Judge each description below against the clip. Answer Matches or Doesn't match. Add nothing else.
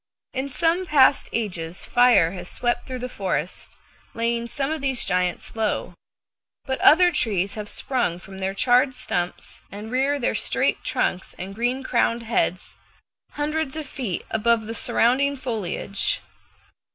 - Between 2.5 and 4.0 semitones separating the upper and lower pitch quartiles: Doesn't match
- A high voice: Matches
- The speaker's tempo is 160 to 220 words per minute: Doesn't match